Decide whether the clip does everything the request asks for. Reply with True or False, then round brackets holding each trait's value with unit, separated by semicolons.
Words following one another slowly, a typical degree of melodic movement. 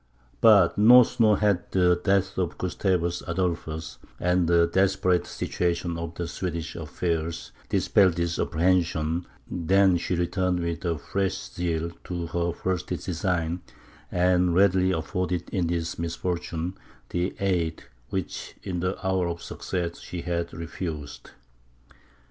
False (125 wpm; 1.6 semitones)